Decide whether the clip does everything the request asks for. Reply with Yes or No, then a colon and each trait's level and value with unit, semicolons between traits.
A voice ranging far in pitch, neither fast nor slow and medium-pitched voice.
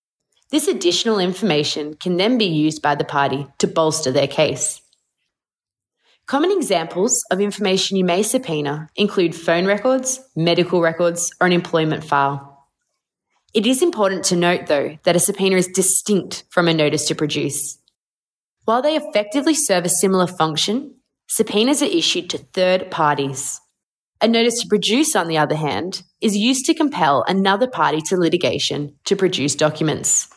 Yes: wide, 5.9 semitones; average, 155 wpm; medium, 180 Hz